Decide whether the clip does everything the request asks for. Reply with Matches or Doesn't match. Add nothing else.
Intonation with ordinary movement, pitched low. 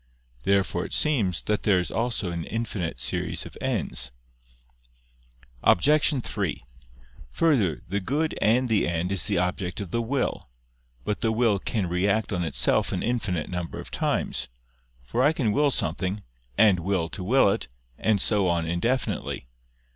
Matches